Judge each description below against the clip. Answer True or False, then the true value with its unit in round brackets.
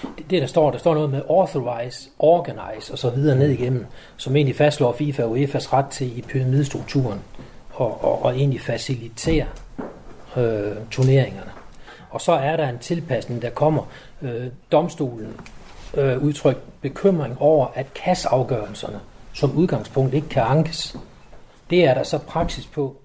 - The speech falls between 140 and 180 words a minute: True (155 wpm)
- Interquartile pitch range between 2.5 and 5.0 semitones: True (3.3 semitones)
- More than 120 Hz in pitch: True (135 Hz)